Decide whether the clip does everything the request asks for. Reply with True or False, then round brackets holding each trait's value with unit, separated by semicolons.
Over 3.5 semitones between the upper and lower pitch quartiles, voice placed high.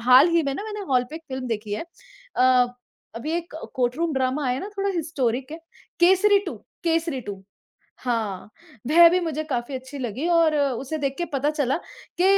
True (4.7 semitones; 280 Hz)